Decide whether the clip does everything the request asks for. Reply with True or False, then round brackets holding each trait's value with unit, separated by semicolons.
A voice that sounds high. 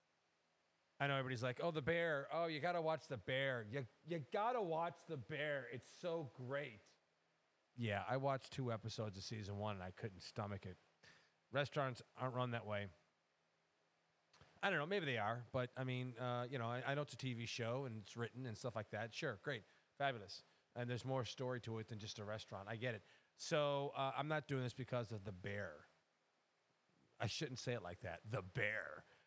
False (125 Hz)